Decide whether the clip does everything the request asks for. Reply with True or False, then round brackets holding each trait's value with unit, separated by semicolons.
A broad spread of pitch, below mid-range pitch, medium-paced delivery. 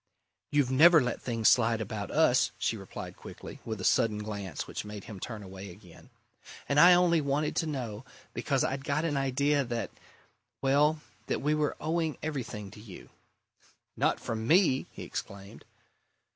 True (5.8 semitones; 130 Hz; 165 wpm)